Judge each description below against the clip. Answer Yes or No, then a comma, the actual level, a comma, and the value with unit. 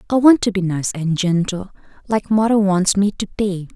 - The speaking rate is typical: No, fast, 210 wpm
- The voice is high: Yes, high, 195 Hz